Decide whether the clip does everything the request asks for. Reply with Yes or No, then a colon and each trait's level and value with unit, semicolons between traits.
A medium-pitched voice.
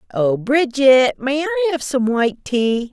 No: very high, 265 Hz